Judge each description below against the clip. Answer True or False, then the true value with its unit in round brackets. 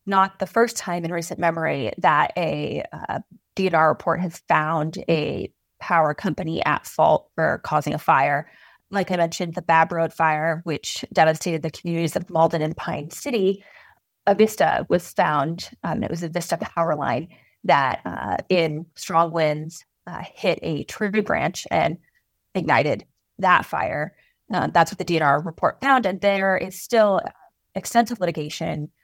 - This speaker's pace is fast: False (160 wpm)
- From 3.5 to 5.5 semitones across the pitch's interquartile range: False (3.0 semitones)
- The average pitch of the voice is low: False (170 Hz)